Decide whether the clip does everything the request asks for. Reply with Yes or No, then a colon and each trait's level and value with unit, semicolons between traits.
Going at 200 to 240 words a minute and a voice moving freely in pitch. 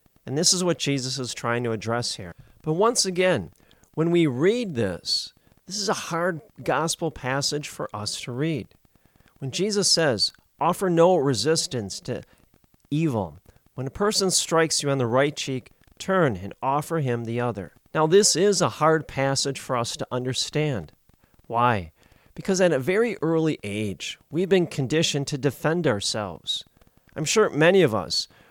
No: average, 165 wpm; wide, 5.8 semitones